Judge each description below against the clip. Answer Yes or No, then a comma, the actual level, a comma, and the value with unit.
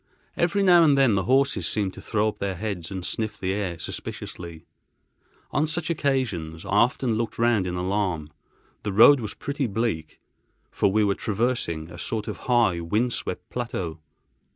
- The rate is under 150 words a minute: No, average, 175 wpm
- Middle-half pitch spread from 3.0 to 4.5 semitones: No, wide, 5.4 semitones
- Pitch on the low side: Yes, low, 105 Hz